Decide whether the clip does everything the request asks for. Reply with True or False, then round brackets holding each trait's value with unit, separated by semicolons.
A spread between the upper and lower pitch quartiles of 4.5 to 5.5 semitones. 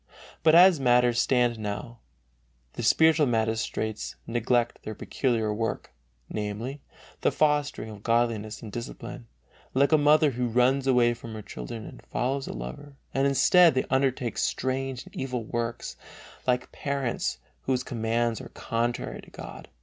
False (3.1 semitones)